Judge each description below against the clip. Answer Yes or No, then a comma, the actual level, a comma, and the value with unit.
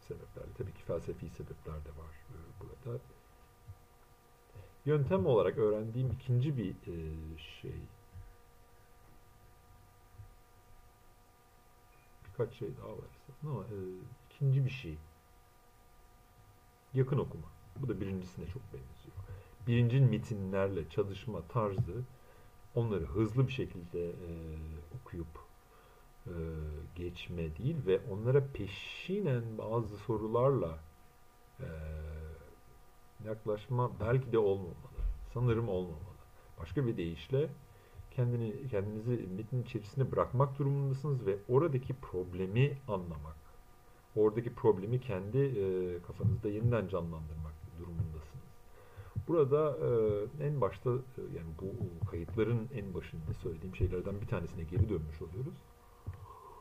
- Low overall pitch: Yes, low, 100 Hz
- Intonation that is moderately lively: No, wide, 6.3 semitones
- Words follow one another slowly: Yes, slow, 90 wpm